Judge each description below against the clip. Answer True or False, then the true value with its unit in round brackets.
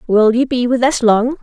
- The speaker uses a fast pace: True (255 wpm)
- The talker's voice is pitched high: True (240 Hz)